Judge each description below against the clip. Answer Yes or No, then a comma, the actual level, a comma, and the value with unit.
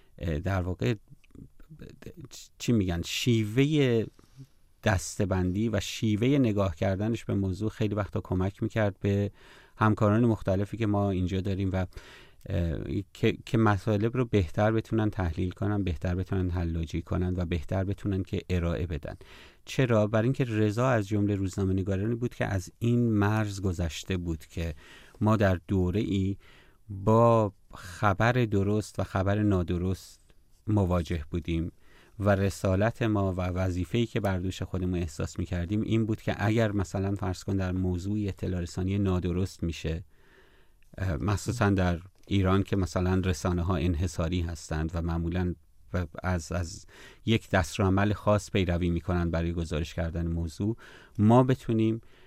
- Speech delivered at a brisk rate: No, average, 135 wpm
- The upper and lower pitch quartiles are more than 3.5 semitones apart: No, average, 3.2 semitones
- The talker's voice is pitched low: Yes, very low, 95 Hz